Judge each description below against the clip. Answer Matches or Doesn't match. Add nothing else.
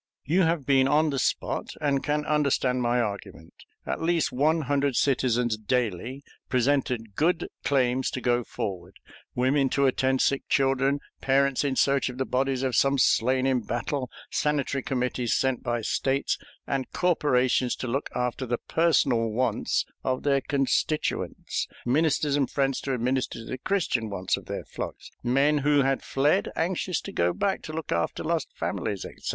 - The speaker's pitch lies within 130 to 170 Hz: Matches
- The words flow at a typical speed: Matches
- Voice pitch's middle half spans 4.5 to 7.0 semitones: Doesn't match